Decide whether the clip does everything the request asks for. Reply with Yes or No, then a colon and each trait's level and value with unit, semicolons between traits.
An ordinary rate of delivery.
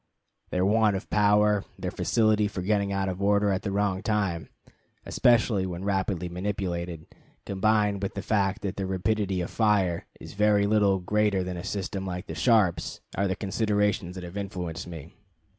Yes: average, 175 wpm